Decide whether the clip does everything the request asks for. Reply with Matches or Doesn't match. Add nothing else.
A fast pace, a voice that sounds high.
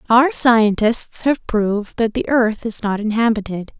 Doesn't match